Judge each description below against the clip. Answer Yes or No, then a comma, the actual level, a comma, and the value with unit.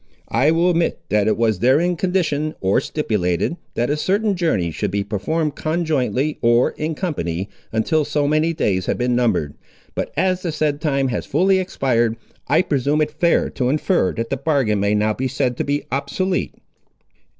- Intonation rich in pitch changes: Yes, wide, 6.1 semitones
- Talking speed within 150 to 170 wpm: No, average, 180 wpm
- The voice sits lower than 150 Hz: Yes, medium, 140 Hz